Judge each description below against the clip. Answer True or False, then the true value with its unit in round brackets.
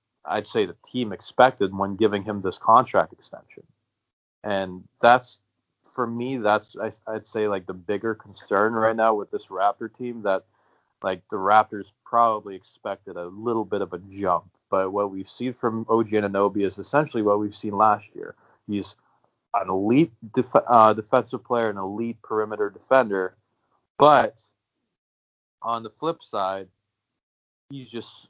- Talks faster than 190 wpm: False (155 wpm)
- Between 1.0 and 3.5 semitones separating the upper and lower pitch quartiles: True (2.7 semitones)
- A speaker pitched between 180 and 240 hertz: False (105 Hz)